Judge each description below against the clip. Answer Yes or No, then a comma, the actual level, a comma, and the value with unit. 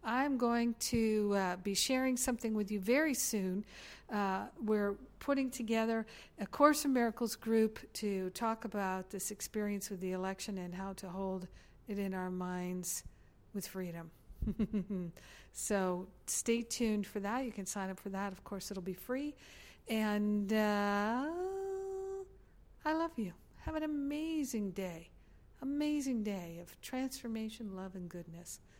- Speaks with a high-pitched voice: Yes, high, 210 Hz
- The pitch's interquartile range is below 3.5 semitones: No, average, 4.2 semitones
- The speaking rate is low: No, average, 145 wpm